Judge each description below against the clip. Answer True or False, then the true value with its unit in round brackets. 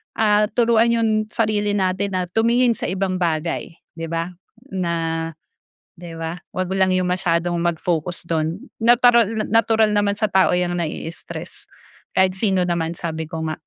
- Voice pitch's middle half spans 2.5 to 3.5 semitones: False (4.0 semitones)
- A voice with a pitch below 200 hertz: True (185 Hz)